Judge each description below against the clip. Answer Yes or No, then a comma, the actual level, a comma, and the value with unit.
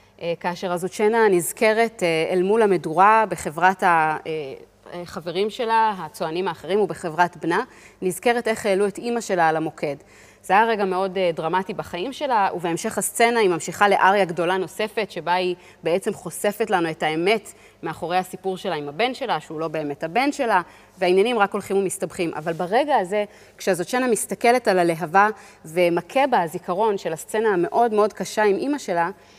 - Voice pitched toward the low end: No, high, 190 Hz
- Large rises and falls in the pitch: No, average, 3.7 semitones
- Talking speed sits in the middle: No, fast, 155 wpm